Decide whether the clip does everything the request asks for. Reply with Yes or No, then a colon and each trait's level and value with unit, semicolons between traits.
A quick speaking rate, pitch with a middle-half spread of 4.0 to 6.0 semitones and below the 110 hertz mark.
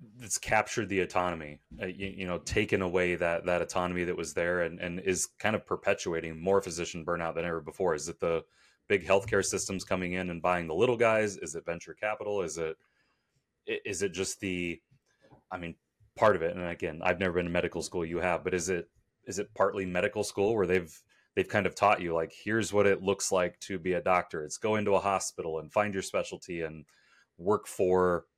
No: fast, 220 wpm; narrow, 2.2 semitones; very low, 90 Hz